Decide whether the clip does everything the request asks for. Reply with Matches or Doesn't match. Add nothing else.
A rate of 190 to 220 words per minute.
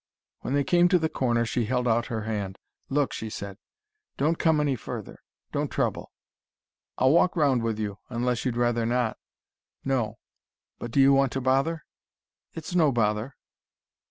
Doesn't match